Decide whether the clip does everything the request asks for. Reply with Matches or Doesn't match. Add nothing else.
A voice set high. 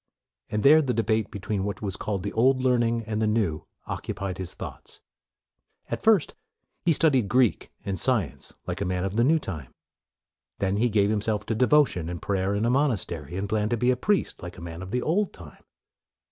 Doesn't match